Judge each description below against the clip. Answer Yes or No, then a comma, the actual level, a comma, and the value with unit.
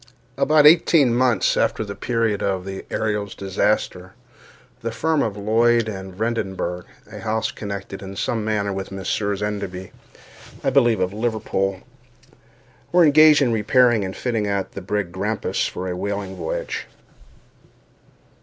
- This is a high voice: No, low, 105 Hz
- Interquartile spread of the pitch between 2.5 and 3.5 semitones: Yes, average, 3.2 semitones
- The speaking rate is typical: Yes, average, 145 wpm